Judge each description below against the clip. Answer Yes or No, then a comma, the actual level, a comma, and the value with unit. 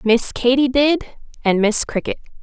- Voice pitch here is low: No, very high, 250 Hz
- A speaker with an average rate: Yes, average, 150 wpm